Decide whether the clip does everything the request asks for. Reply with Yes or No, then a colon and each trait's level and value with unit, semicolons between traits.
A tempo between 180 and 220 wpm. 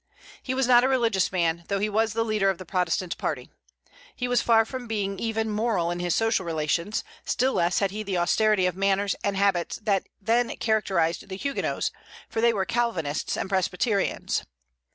Yes: average, 190 wpm